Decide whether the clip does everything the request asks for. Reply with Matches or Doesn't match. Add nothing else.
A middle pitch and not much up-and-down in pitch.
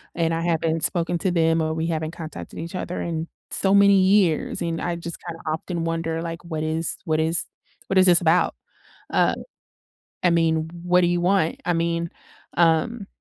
Matches